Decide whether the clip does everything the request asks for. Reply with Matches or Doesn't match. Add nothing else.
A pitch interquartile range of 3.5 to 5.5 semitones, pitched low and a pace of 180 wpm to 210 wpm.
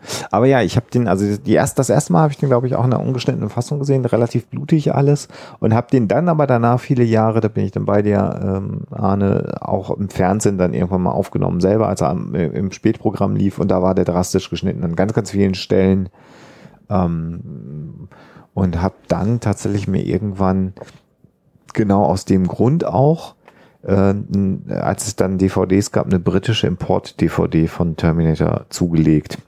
Matches